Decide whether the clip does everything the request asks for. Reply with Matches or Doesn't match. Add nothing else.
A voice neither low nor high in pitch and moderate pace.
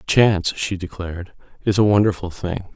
Doesn't match